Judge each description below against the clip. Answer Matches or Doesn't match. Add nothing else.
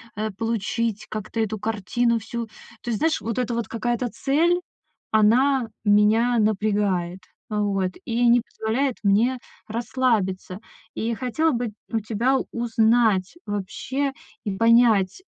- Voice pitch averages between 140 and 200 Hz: Doesn't match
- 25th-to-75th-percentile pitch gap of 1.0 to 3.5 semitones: Matches